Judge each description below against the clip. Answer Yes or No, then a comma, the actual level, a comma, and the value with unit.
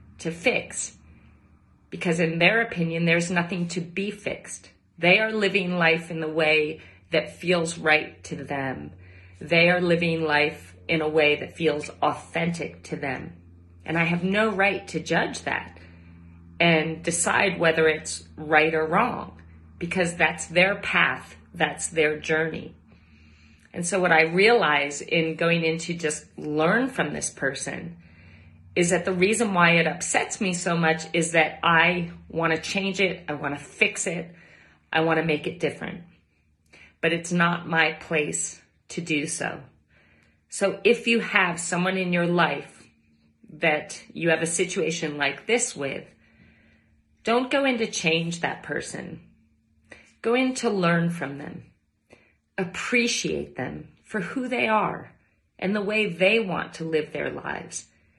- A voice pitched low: No, medium, 165 Hz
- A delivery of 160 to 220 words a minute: No, average, 150 wpm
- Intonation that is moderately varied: Yes, average, 3.1 semitones